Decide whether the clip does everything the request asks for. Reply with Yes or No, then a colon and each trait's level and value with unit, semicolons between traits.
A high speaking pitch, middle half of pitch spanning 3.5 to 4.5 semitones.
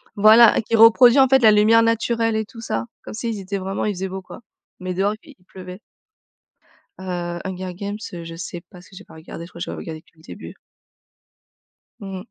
Yes: high, 195 Hz; average, 3.8 semitones